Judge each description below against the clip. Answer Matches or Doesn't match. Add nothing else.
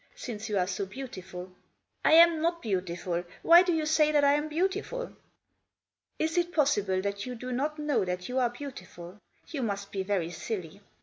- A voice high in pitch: Matches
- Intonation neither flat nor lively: Doesn't match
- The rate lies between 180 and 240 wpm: Matches